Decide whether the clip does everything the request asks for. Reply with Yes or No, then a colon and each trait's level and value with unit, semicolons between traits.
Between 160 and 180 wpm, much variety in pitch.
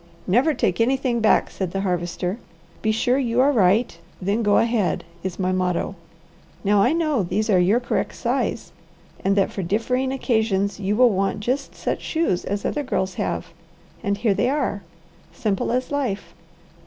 No: average, 170 wpm; average, 4.5 semitones